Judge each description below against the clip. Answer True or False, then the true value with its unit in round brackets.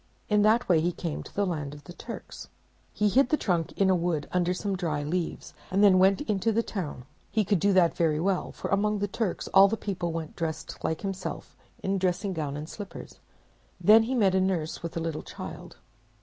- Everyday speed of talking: False (220 wpm)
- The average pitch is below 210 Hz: True (185 Hz)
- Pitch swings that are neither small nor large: True (3.6 semitones)